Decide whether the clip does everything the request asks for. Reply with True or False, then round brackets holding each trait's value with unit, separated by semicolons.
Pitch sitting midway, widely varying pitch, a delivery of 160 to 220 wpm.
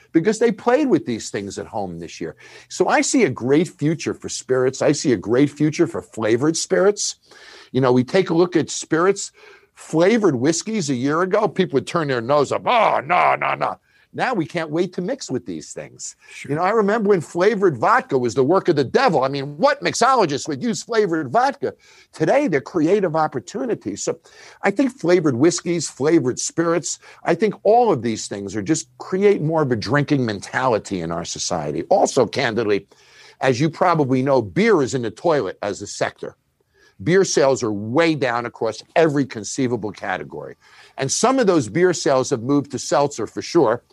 True (165 Hz; 7.4 semitones; 195 wpm)